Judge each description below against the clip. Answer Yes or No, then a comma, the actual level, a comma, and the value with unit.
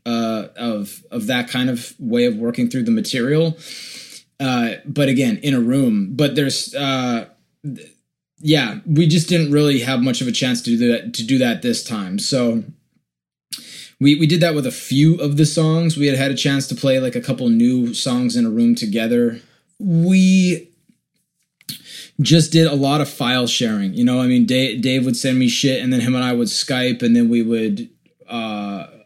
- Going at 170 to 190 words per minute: No, average, 200 wpm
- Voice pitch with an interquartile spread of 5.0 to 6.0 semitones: Yes, average, 5.3 semitones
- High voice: No, low, 135 Hz